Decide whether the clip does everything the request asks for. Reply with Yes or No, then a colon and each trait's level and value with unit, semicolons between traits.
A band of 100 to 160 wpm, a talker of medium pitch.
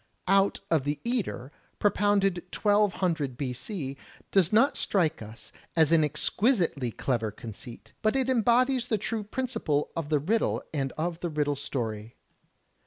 Yes: average, 140 wpm; medium, 165 Hz